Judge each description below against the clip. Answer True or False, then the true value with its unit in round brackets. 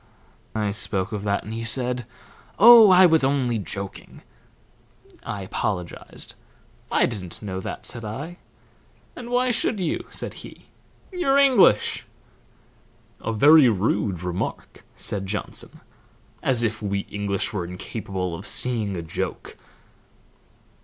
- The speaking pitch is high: False (110 Hz)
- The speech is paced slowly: True (125 wpm)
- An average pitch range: False (6.4 semitones)